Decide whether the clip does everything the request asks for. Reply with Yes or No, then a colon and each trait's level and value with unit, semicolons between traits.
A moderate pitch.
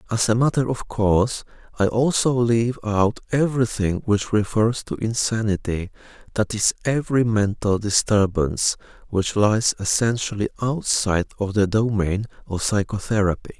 No: low, 110 Hz